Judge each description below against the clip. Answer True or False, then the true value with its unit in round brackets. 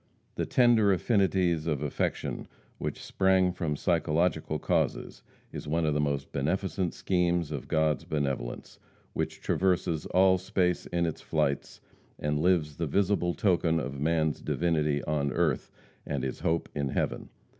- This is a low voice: True (80 Hz)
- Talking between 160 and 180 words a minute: False (145 wpm)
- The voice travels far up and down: False (3.5 semitones)